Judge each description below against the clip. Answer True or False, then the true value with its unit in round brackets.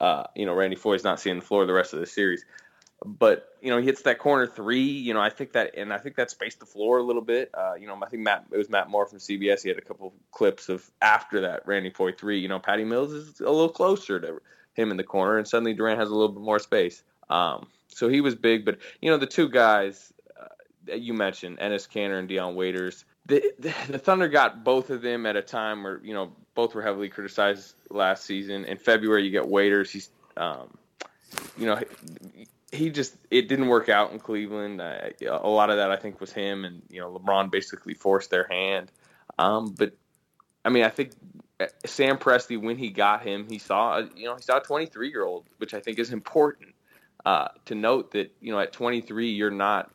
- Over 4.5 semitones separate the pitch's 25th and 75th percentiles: False (4.2 semitones)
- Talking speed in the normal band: False (235 wpm)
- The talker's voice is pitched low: True (110 Hz)